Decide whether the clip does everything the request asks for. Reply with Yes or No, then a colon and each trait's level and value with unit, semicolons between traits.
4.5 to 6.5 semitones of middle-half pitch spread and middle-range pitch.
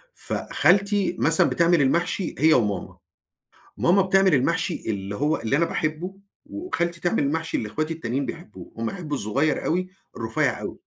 Yes: average, 4.8 semitones; medium, 165 Hz